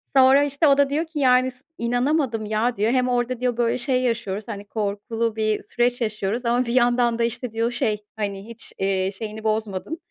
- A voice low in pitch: No, high, 235 Hz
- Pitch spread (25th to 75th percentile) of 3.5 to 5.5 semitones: No, average, 2.7 semitones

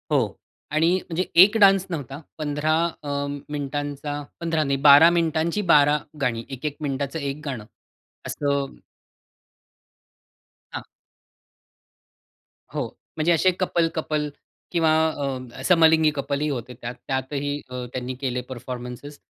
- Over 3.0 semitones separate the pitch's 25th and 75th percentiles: No, average, 2.7 semitones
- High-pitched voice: No, medium, 145 Hz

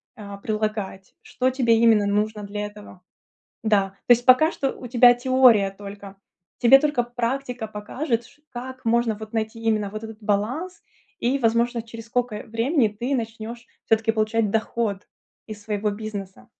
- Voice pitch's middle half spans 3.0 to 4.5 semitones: No, narrow, 2.5 semitones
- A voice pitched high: Yes, high, 225 Hz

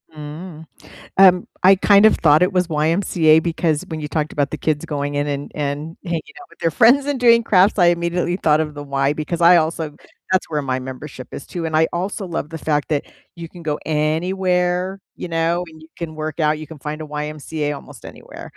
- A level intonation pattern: No, average, 3.0 semitones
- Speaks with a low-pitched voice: No, medium, 160 Hz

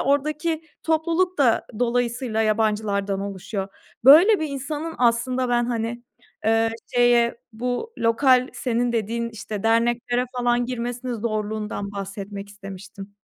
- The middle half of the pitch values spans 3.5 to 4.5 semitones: No, average, 2.9 semitones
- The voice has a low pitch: No, high, 235 Hz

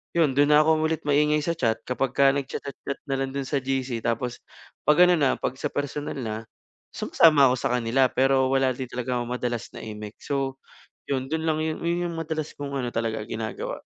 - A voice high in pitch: No, low, 135 Hz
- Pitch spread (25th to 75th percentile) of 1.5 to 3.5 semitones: Yes, average, 3.2 semitones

